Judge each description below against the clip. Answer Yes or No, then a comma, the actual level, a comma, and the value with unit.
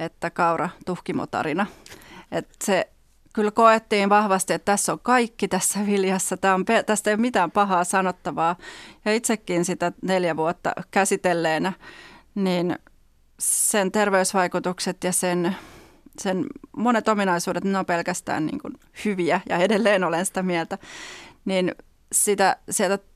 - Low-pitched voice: No, high, 190 Hz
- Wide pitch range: No, average, 2.7 semitones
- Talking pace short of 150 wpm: Yes, average, 130 wpm